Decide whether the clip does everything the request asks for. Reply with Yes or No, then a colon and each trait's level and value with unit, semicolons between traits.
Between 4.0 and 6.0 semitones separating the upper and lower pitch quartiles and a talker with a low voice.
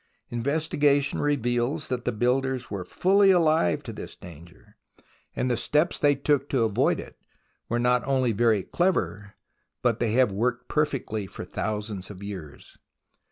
Yes: average, 5.2 semitones; low, 125 Hz